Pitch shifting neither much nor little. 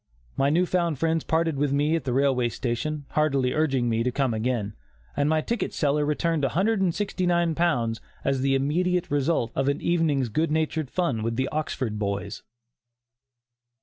Yes: average, 4.3 semitones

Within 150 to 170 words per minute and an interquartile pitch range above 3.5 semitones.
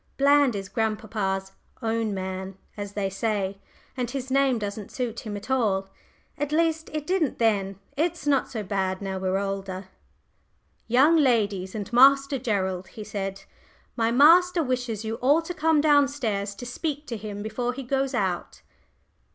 Yes: average, 160 wpm; wide, 5.6 semitones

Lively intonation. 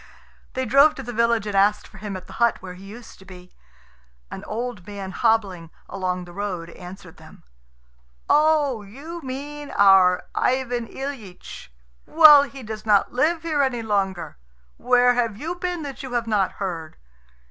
Yes: wide, 5.7 semitones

